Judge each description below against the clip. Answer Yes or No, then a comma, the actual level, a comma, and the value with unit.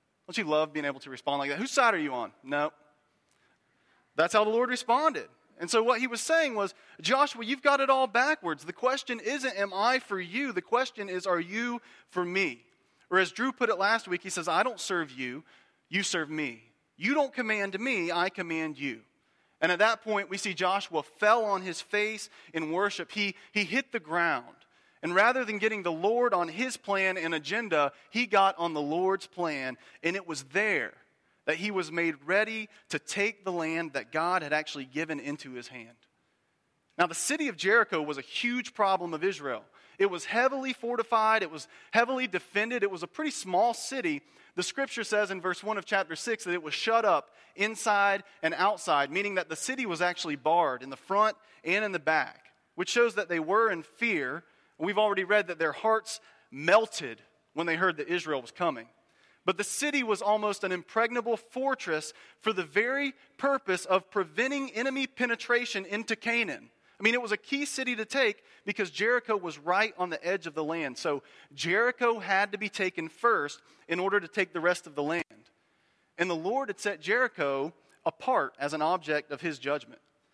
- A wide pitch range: Yes, wide, 5.7 semitones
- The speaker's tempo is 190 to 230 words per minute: Yes, average, 200 wpm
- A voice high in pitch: Yes, high, 200 Hz